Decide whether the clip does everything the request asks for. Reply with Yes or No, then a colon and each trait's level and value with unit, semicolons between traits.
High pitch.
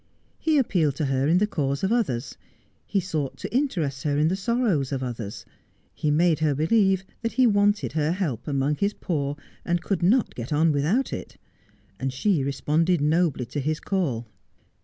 No: medium, 155 Hz